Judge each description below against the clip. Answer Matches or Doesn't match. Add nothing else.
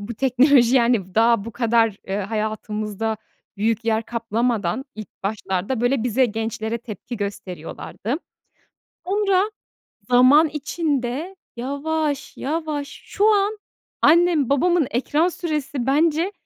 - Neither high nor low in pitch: Doesn't match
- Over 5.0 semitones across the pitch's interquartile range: Matches